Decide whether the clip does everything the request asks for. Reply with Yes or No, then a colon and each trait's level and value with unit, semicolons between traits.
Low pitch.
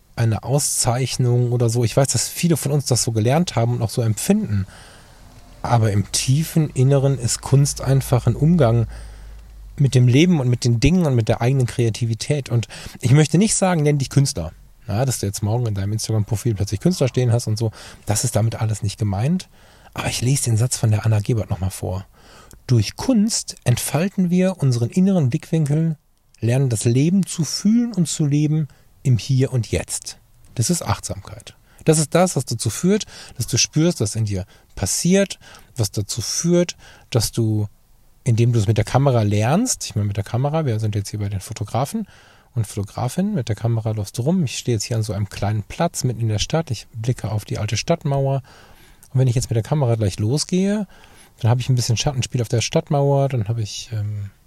Yes: low, 120 Hz